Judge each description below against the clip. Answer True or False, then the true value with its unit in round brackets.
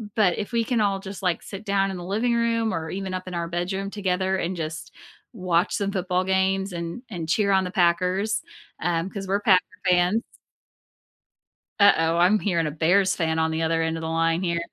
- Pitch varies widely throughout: False (2.7 semitones)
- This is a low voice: False (185 Hz)